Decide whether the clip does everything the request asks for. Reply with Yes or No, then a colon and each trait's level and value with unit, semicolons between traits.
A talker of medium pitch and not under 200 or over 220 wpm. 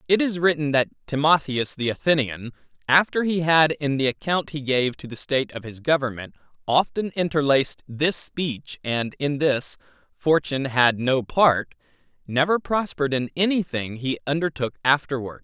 No: medium, 145 Hz; average, 150 wpm